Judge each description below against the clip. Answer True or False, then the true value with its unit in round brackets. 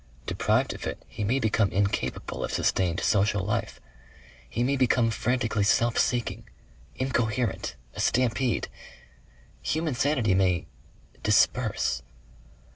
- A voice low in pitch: True (115 Hz)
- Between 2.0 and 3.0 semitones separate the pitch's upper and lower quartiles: False (4.0 semitones)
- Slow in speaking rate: True (115 wpm)